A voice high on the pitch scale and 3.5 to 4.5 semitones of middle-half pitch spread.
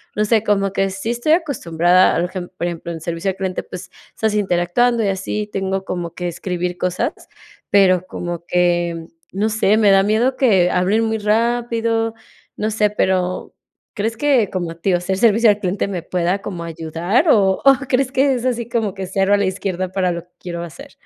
Yes: high, 195 Hz; average, 3.8 semitones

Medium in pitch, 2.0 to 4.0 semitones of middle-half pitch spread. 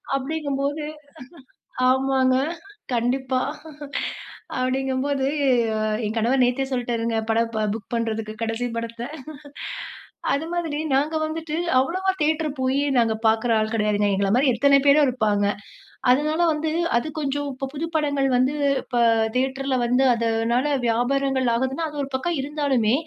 No: very high, 260 Hz; average, 3.6 semitones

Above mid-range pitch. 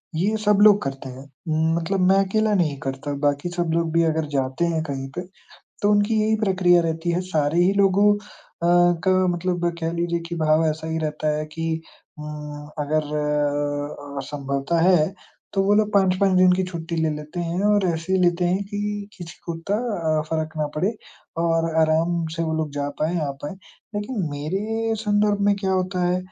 No: medium, 170 Hz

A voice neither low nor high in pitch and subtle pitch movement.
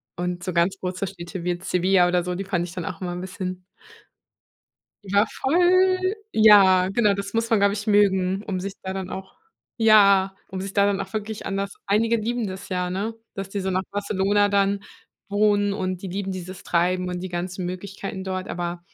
No: high, 195 Hz; narrow, 1.8 semitones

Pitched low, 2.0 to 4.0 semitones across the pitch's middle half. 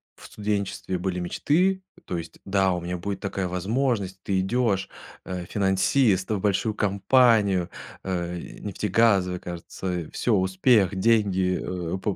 Yes: very low, 95 Hz; narrow, 2.6 semitones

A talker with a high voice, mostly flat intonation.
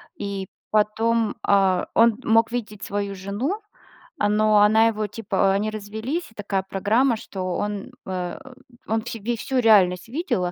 Yes: high, 210 Hz; narrow, 2.3 semitones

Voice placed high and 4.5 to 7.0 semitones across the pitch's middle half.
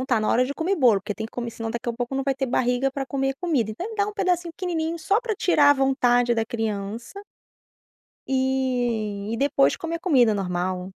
Yes: very high, 255 Hz; wide, 5.6 semitones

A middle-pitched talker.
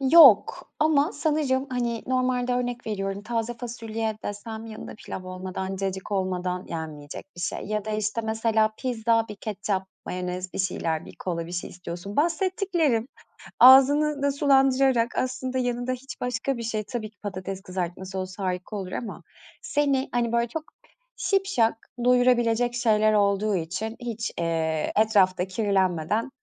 No: high, 220 Hz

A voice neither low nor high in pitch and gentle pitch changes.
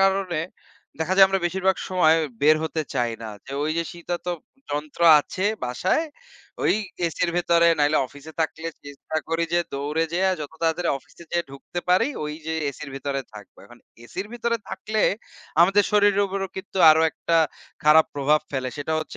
No: medium, 165 Hz; average, 4.2 semitones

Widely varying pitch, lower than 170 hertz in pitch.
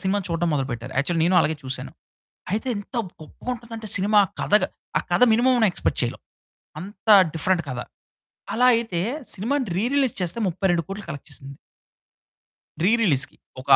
No: wide, 5.9 semitones; high, 190 Hz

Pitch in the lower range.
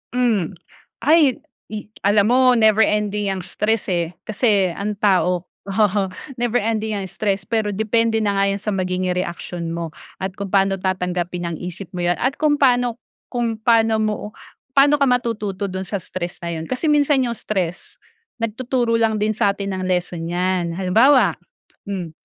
No: high, 205 Hz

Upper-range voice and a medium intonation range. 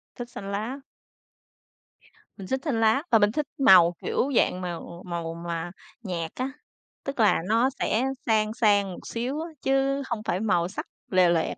No: high, 215 Hz; wide, 5.9 semitones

